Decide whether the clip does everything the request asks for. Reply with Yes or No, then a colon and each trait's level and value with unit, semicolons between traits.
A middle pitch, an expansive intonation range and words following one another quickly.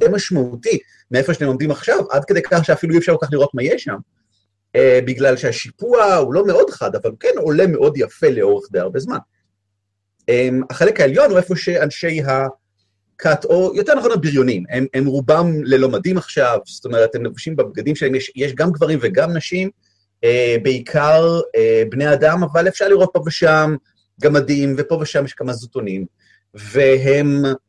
Yes: medium, 145 Hz; wide, 5.8 semitones; fast, 165 wpm